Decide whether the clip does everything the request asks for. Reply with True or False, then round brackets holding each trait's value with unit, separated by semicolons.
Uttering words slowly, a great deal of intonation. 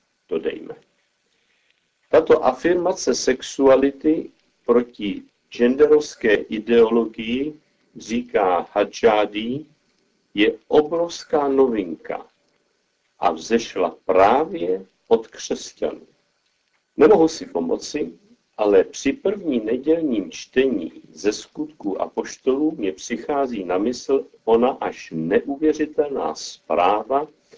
True (85 wpm; 8.0 semitones)